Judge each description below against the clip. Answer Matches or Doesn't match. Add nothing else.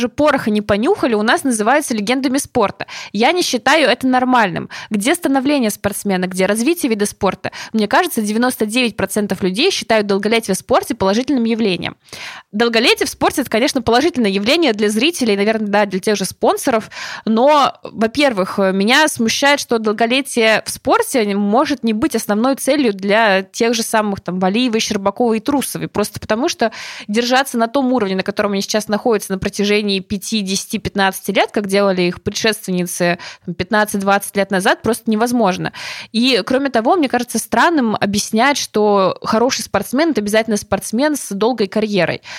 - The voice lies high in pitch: Matches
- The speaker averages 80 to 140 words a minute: Doesn't match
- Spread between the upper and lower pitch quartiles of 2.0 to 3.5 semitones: Doesn't match